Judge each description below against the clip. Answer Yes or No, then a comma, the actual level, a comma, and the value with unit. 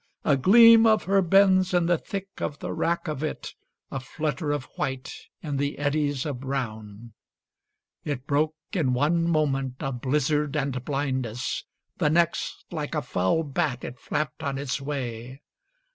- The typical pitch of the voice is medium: Yes, medium, 145 Hz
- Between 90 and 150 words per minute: No, average, 160 wpm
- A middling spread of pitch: Yes, average, 3.8 semitones